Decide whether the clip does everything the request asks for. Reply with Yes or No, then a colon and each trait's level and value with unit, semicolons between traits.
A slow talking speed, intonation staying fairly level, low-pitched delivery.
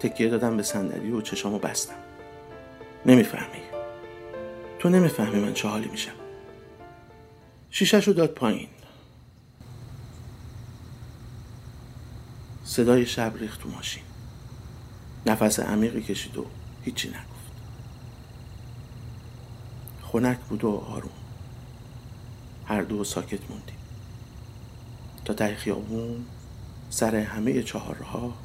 Yes: slow, 90 wpm; narrow, 1.6 semitones; low, 115 Hz